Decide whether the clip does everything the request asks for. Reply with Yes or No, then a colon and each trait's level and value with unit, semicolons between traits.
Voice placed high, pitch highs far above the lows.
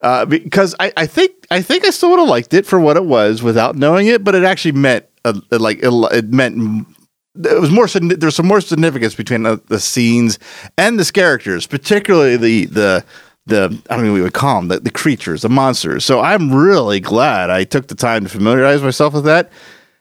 No: low, 135 Hz; wide, 8.0 semitones